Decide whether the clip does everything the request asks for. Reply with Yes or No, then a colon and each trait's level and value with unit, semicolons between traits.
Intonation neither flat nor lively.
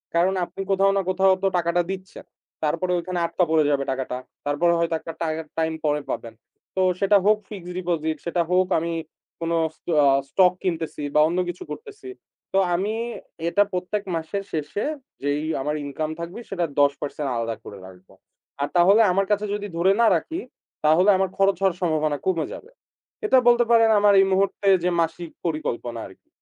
Yes: average, 4.0 semitones